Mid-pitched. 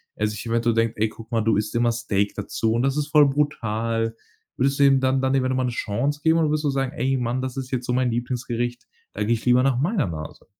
No: low, 125 Hz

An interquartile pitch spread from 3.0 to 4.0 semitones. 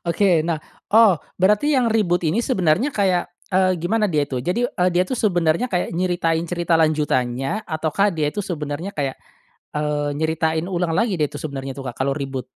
No: average, 4.6 semitones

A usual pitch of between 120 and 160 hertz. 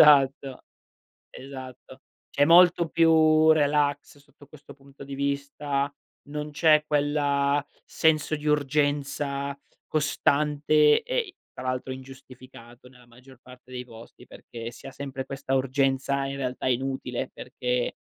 Yes: medium, 140 Hz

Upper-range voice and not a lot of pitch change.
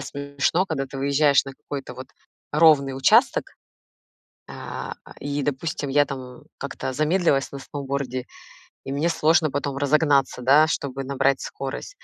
No: medium, 140 Hz; narrow, 1.8 semitones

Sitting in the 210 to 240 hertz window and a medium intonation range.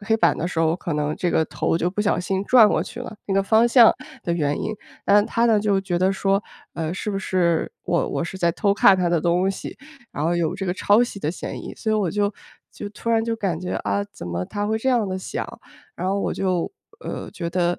No: high, 190 Hz; average, 3.4 semitones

